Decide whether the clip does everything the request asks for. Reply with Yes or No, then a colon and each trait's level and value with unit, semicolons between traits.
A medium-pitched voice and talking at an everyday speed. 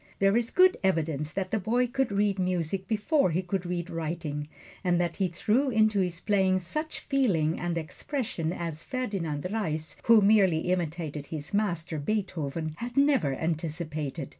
Yes: medium, 180 Hz; average, 160 wpm